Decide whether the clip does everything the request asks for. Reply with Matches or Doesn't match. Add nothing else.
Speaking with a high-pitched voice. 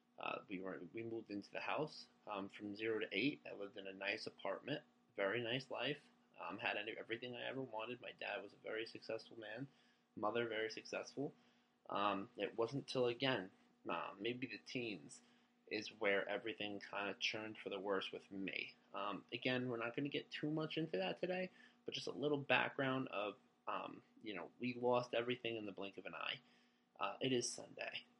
Doesn't match